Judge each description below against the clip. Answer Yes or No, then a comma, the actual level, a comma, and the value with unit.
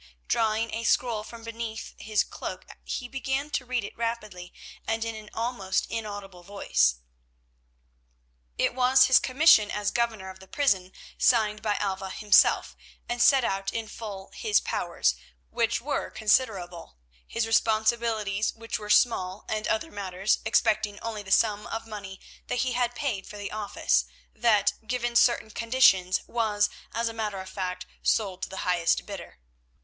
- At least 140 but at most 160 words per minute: Yes, average, 155 wpm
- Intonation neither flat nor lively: Yes, average, 3.0 semitones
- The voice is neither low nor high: No, high, 220 Hz